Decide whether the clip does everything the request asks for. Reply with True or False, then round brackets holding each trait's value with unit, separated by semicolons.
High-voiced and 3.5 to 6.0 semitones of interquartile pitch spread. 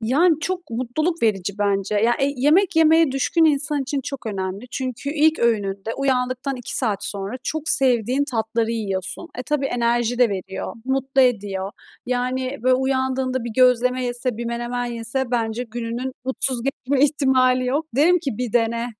False (250 Hz; 3.0 semitones)